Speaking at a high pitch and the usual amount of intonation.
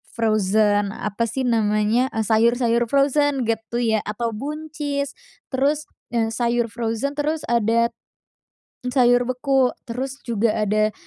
Yes: high, 235 Hz; average, 3.3 semitones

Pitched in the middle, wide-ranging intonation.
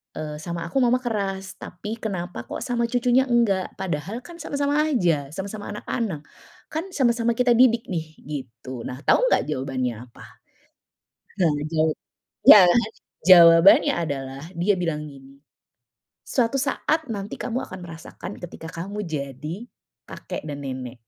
Yes: medium, 180 Hz; wide, 7.7 semitones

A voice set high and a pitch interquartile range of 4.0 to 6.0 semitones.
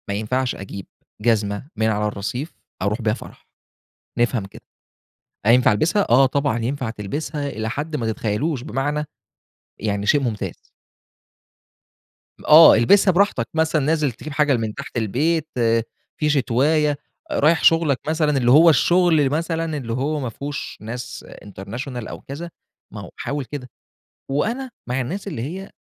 No: low, 135 Hz; average, 5.2 semitones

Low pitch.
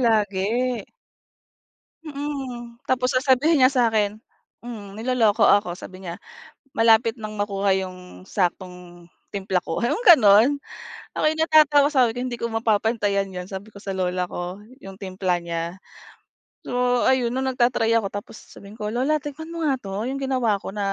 No: high, 220 Hz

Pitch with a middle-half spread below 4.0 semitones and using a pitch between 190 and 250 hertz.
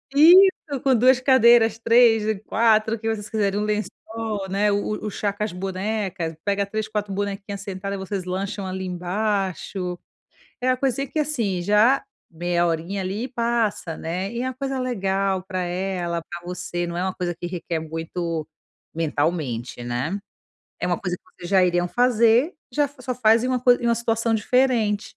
No: average, 4.3 semitones; high, 205 Hz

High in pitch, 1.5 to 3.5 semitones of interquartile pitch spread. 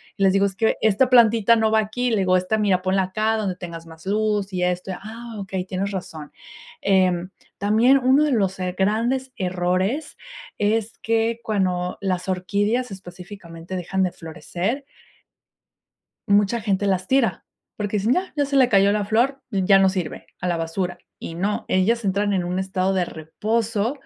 Yes: high, 200 Hz; average, 3.2 semitones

